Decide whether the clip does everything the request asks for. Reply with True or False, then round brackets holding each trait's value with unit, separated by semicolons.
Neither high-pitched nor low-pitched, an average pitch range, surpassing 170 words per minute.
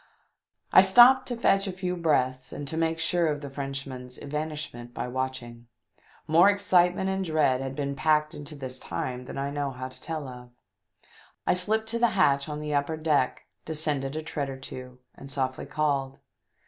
True (145 Hz; 3.7 semitones; 185 wpm)